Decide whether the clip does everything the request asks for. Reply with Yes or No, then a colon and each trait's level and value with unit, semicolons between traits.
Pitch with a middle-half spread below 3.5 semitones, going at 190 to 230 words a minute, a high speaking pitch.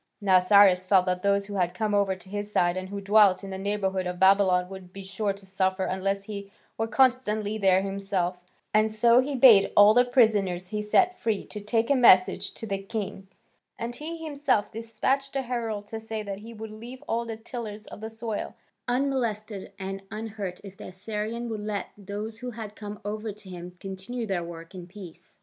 Yes: average, 2.7 semitones; average, 200 wpm; high, 205 Hz